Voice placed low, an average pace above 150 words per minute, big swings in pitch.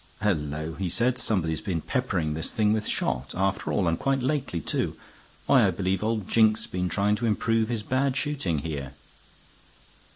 Yes: low, 100 Hz; average, 175 wpm; wide, 5.7 semitones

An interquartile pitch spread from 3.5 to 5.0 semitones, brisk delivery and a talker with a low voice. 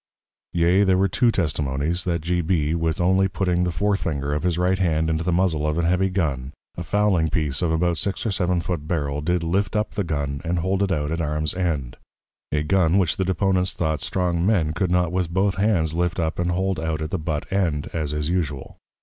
No: average, 3.1 semitones; fast, 225 wpm; very low, 85 Hz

